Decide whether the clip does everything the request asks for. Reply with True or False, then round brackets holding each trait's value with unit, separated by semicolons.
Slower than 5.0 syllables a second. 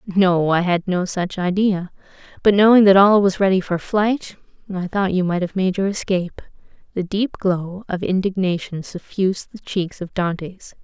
True (4.7 syllables/s)